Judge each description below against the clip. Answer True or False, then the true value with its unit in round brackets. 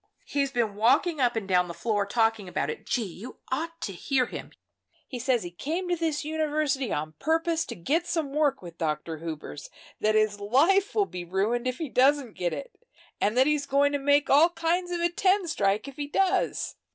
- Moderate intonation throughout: False (7.5 semitones)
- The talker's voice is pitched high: True (265 Hz)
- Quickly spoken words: True (210 wpm)